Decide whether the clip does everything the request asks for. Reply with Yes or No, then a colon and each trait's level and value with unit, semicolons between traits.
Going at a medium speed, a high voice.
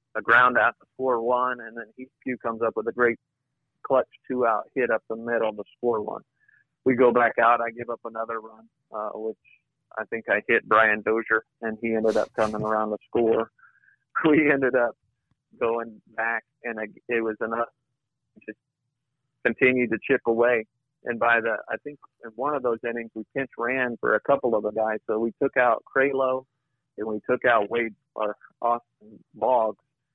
No: average, 195 wpm; low, 120 Hz